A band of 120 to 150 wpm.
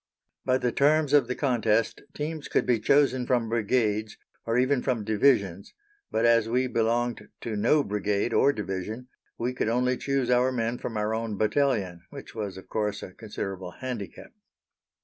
No: average, 170 wpm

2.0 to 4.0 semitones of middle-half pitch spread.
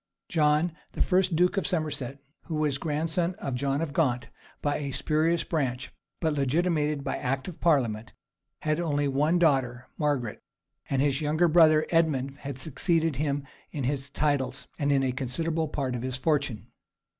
Yes: average, 3.1 semitones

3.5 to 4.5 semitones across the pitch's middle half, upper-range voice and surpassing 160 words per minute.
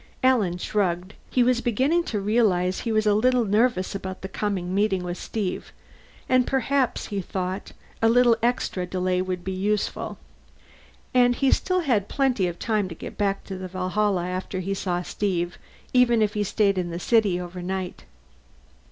Yes: average, 4.2 semitones; high, 200 Hz; average, 170 wpm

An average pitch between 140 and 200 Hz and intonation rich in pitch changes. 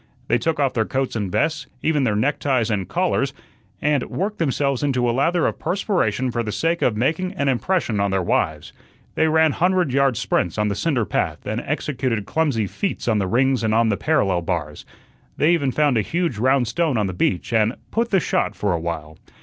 No: low, 130 Hz; wide, 6.8 semitones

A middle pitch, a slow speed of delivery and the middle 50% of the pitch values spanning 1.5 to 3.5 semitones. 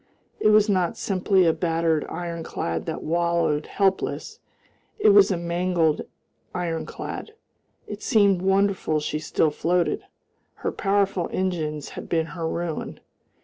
Yes: medium, 175 Hz; slow, 125 wpm; average, 3.1 semitones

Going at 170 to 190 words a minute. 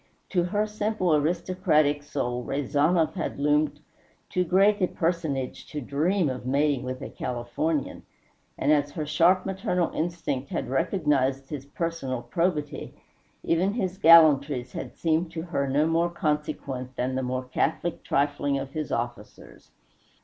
No: average, 140 wpm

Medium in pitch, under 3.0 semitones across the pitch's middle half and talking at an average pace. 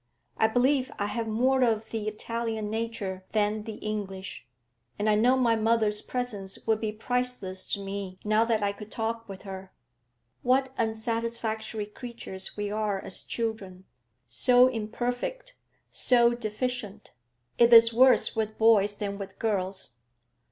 No: high, 220 Hz; narrow, 2.4 semitones; average, 145 wpm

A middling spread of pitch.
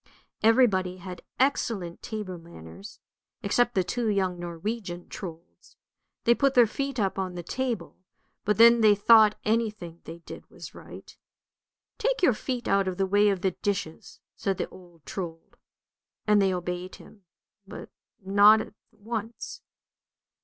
Yes: average, 4.0 semitones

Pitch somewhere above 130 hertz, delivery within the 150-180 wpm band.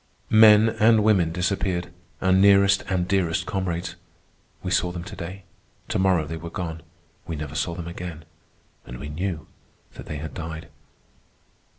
No: very low, 90 Hz; average, 160 wpm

